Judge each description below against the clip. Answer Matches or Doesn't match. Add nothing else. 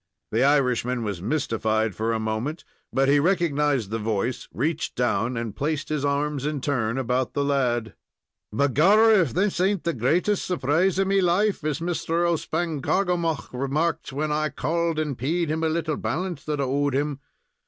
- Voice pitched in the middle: Matches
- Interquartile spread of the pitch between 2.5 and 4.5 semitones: Doesn't match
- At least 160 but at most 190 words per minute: Matches